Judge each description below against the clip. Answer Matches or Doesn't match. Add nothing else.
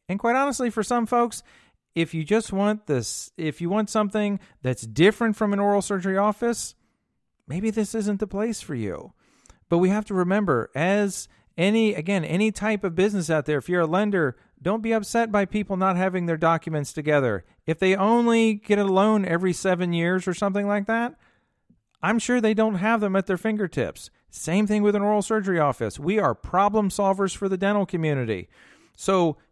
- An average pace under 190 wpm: Doesn't match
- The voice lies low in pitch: Doesn't match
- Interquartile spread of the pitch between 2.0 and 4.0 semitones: Matches